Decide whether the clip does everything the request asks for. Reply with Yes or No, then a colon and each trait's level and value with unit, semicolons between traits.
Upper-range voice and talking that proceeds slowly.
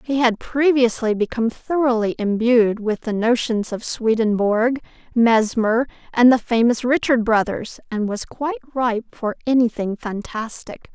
Yes: high, 235 Hz; slow, 130 wpm